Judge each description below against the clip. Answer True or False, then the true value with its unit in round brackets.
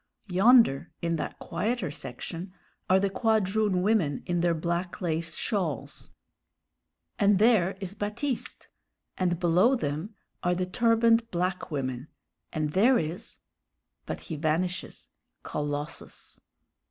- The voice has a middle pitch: True (180 Hz)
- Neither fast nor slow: False (115 wpm)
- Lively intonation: False (4.5 semitones)